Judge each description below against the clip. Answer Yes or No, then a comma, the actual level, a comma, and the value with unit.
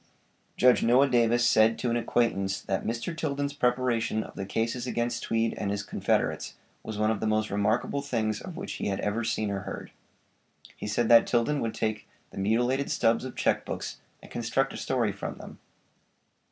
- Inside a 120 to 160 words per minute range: No, average, 190 wpm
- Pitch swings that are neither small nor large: No, narrow, 2.3 semitones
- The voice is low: Yes, low, 115 Hz